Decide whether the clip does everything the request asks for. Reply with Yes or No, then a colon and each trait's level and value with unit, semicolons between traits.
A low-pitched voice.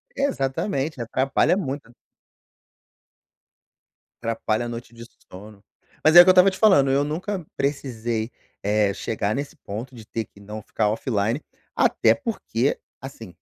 Yes: low, 125 Hz